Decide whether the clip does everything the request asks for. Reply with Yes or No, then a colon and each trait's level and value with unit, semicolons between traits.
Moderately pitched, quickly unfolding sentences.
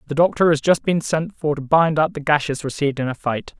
Yes: medium, 150 Hz; fast, 265 wpm